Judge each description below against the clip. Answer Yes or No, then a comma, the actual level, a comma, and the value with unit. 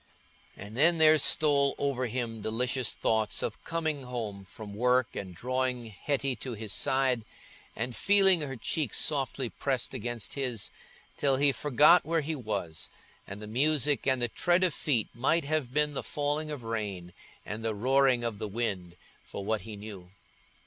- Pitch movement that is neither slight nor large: Yes, average, 4.7 semitones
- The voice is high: No, low, 125 Hz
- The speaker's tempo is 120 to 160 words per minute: No, average, 170 wpm